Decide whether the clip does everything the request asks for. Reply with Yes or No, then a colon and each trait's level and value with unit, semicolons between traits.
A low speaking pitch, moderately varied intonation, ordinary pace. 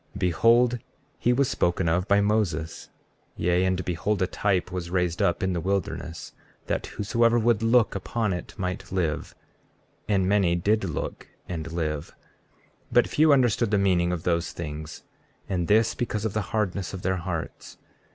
Yes: very low, 95 Hz; average, 3.6 semitones; average, 170 wpm